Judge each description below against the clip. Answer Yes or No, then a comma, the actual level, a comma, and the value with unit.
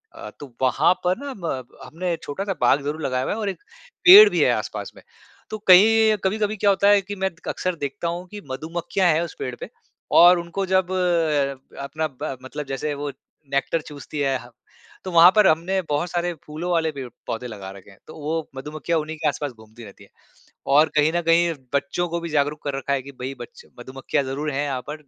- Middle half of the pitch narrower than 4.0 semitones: No, average, 4.7 semitones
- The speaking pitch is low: No, medium, 155 Hz